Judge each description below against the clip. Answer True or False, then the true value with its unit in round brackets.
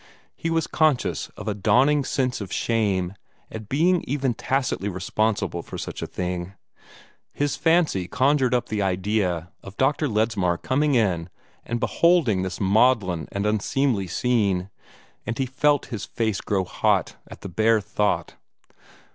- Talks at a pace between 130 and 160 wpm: True (145 wpm)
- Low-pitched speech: True (110 Hz)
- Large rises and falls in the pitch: True (5.7 semitones)